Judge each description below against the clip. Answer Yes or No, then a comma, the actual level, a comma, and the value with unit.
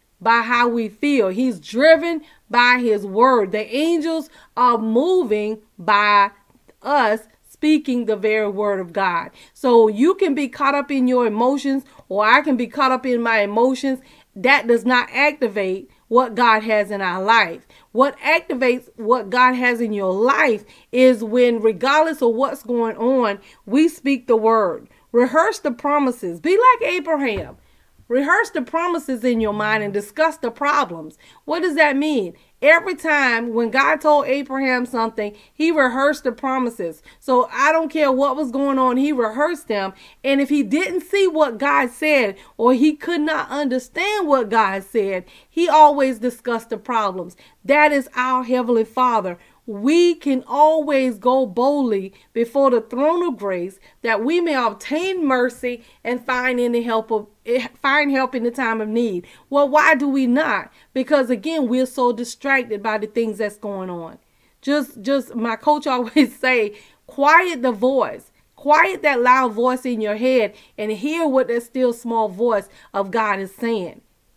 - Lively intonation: No, average, 4.3 semitones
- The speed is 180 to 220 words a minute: No, average, 165 wpm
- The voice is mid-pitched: No, very high, 250 Hz